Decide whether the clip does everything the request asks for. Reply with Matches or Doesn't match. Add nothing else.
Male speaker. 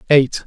Matches